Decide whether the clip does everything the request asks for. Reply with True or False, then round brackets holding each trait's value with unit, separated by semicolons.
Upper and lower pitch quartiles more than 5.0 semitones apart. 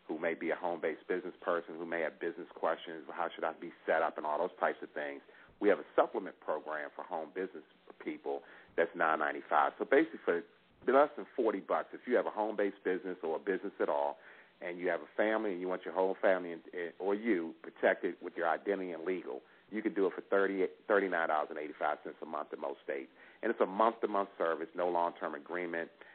False (2.9 semitones)